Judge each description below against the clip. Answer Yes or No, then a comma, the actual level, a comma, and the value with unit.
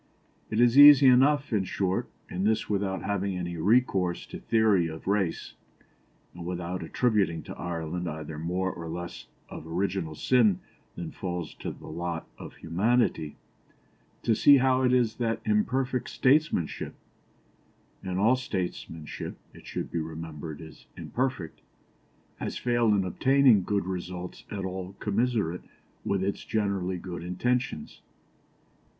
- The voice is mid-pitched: No, very low, 95 Hz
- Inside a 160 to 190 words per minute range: No, slow, 135 wpm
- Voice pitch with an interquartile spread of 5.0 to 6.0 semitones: Yes, wide, 5.5 semitones